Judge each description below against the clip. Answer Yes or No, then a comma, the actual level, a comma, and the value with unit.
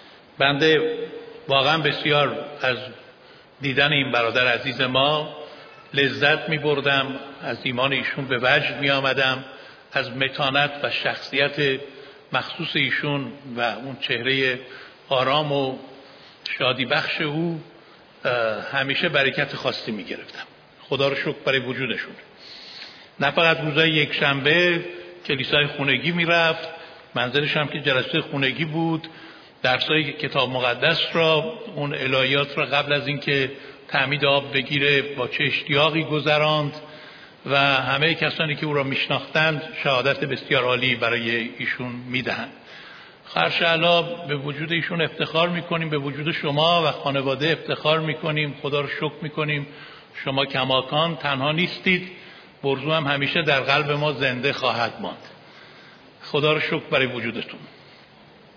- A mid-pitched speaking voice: Yes, medium, 145 Hz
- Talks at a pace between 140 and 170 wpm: No, average, 125 wpm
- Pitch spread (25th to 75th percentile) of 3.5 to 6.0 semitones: No, narrow, 2.5 semitones